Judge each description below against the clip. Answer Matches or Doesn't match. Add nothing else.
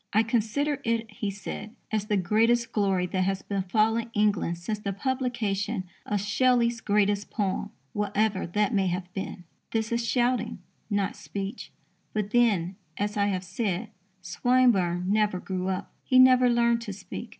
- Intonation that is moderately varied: Matches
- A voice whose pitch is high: Matches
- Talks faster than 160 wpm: Doesn't match